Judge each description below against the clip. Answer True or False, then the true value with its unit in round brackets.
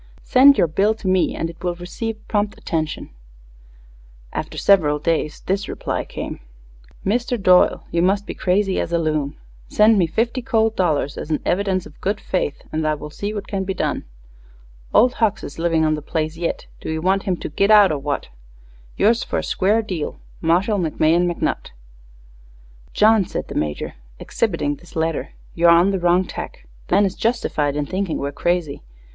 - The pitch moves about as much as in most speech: True (4.4 semitones)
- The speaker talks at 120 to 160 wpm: False (185 wpm)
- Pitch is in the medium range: True (180 Hz)